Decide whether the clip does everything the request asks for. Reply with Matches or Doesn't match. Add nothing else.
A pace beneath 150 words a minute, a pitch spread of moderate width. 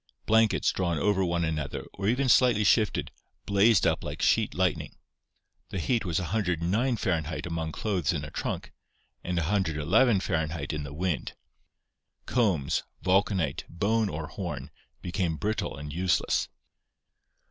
Matches